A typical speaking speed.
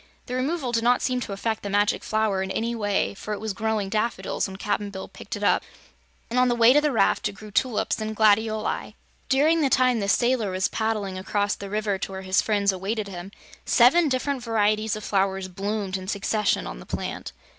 No: fast, 215 wpm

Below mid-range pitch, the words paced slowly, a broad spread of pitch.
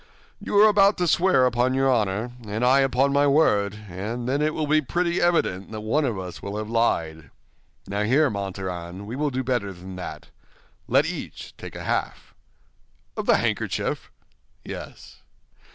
No: low, 120 Hz; average, 170 wpm; wide, 6.2 semitones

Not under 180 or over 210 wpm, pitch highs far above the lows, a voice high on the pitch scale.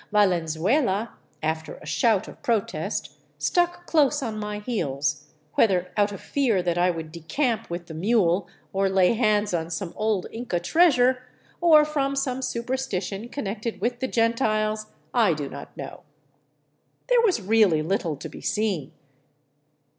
No: average, 155 wpm; wide, 5.7 semitones; high, 210 Hz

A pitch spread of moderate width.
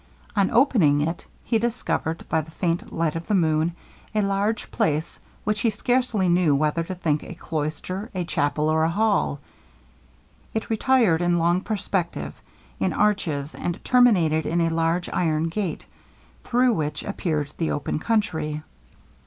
Yes: average, 4.9 semitones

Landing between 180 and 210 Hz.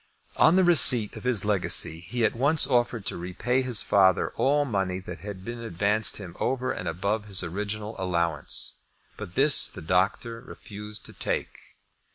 No: low, 105 Hz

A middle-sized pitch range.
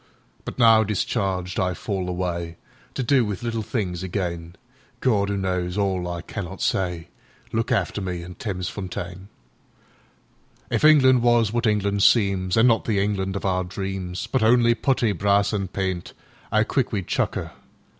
Yes: average, 3.7 semitones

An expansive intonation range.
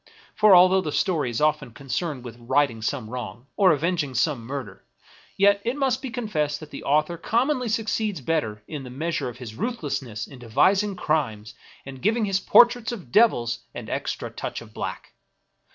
Yes: wide, 8.4 semitones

